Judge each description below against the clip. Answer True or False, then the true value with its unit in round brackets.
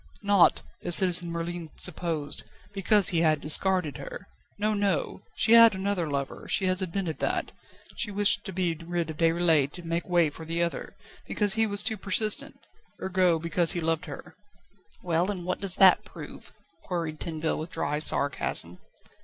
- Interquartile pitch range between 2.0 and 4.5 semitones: True (2.9 semitones)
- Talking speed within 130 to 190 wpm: True (170 wpm)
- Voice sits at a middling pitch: True (175 Hz)